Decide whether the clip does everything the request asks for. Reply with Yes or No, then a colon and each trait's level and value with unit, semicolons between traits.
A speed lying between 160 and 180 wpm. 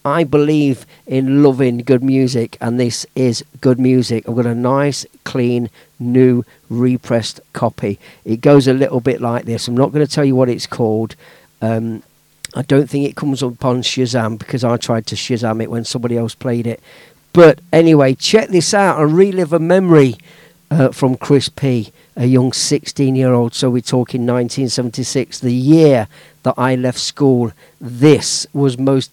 Yes: average, 175 wpm